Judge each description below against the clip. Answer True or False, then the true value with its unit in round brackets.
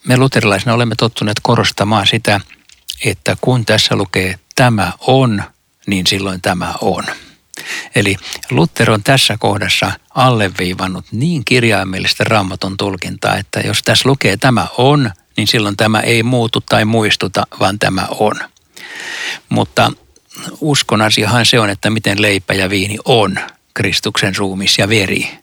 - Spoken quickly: False (130 wpm)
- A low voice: True (110 Hz)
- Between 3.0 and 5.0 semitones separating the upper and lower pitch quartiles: True (3.7 semitones)